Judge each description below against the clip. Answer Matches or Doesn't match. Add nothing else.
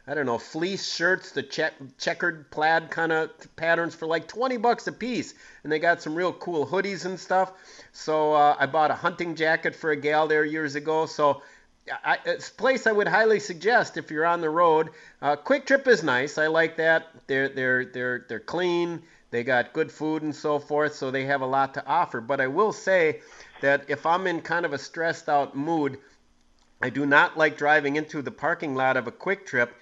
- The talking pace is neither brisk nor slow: Doesn't match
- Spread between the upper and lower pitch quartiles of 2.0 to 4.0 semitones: Matches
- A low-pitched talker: Doesn't match